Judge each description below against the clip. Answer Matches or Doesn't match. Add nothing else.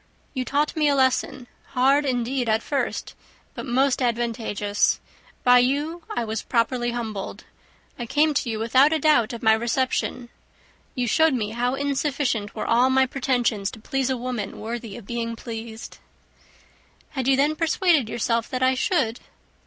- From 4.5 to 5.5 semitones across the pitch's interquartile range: Doesn't match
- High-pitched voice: Matches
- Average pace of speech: Matches